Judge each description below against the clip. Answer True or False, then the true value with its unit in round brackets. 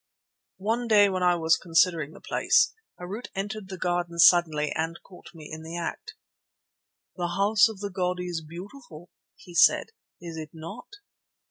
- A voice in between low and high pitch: True (175 Hz)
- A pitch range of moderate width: True (3.2 semitones)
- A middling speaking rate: True (160 wpm)